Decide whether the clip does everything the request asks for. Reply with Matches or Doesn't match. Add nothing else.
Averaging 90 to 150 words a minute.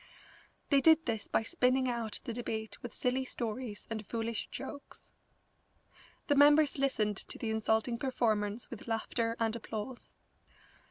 Matches